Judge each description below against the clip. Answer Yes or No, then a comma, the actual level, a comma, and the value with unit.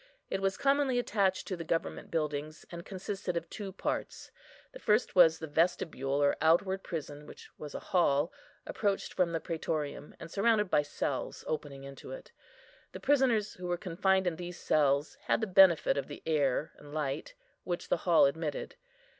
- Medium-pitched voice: Yes, medium, 170 Hz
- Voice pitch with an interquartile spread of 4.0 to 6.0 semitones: Yes, average, 4.4 semitones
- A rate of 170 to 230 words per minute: Yes, average, 175 wpm